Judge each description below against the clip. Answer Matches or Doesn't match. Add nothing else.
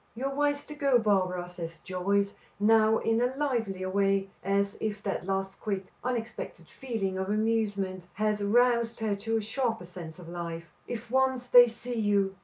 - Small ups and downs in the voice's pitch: Doesn't match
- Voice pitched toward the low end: Doesn't match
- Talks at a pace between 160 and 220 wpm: Matches